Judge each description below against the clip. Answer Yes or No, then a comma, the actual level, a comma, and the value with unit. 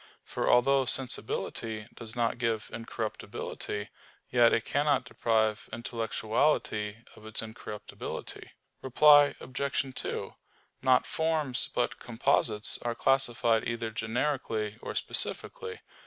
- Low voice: Yes, low, 120 Hz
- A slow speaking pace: Yes, slow, 105 wpm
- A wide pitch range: No, average, 3.3 semitones